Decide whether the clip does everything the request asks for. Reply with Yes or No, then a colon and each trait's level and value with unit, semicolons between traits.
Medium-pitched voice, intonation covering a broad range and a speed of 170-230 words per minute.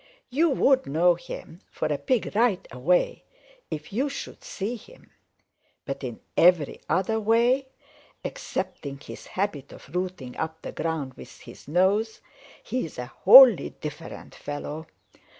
No: medium, 180 Hz; wide, 7.1 semitones; average, 140 wpm